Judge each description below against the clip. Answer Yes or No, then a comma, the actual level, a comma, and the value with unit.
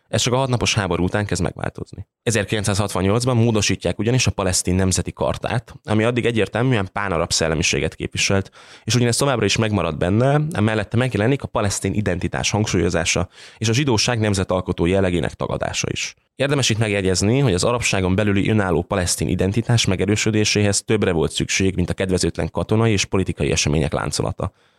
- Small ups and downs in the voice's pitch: No, average, 3.9 semitones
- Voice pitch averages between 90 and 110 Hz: Yes, low, 100 Hz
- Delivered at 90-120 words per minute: No, average, 150 wpm